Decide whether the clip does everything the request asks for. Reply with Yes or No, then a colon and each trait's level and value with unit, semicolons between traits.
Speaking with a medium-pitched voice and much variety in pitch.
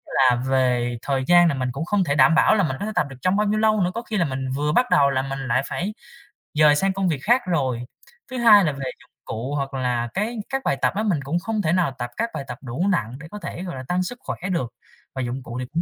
Yes: medium, 150 Hz; wide, 6.8 semitones